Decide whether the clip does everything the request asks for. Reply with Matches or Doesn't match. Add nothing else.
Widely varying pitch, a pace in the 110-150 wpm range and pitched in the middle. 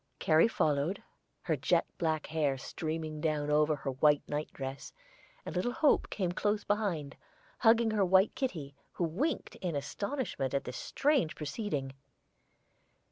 Matches